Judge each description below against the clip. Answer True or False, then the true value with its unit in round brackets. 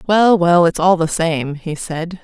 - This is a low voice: False (170 Hz)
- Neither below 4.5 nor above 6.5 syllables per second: False (3.9 syllables/s)